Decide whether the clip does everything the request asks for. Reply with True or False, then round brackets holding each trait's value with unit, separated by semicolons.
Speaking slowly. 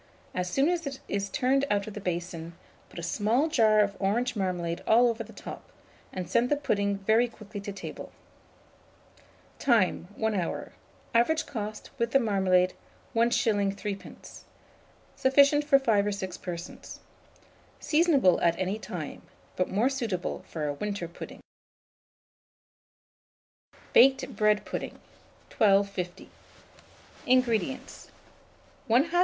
True (130 wpm)